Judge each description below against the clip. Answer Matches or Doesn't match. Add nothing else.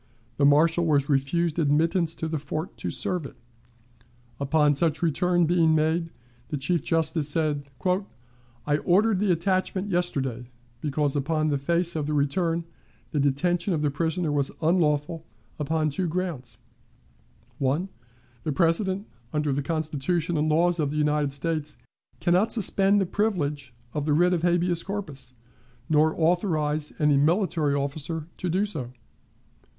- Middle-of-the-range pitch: Matches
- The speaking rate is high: Doesn't match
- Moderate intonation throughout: Matches